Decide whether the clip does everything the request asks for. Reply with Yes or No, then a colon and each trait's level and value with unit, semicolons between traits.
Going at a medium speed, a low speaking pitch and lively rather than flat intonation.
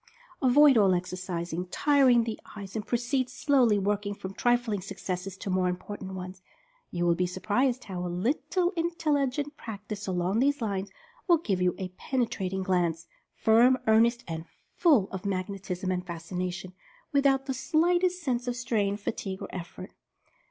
No: average, 165 wpm; high, 205 Hz; wide, 5.7 semitones